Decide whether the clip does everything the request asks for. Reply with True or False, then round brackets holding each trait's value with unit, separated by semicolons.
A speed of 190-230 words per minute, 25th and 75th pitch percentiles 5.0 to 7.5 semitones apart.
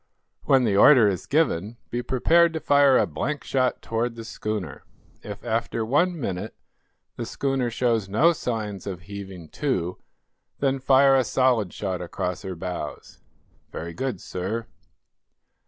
False (145 wpm; 5.6 semitones)